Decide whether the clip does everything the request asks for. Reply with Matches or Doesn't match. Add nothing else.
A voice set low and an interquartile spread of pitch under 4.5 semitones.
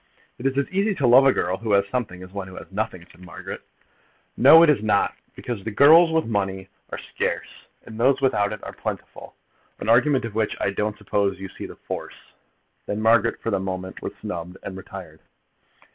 Doesn't match